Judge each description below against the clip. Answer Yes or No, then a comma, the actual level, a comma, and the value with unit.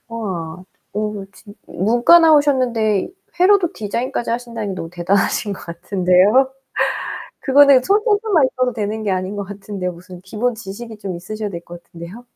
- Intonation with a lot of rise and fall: No, average, 4.9 semitones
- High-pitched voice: Yes, high, 215 Hz